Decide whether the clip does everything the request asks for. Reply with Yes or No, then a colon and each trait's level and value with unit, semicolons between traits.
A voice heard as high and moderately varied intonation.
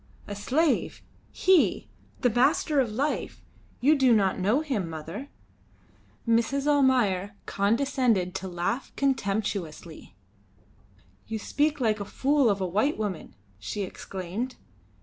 No: high, 220 Hz; wide, 6.0 semitones